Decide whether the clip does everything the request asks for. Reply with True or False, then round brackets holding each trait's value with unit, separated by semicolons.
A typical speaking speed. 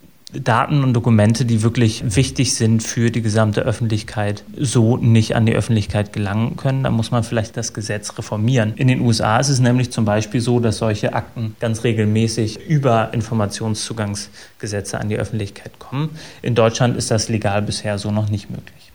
True (175 wpm)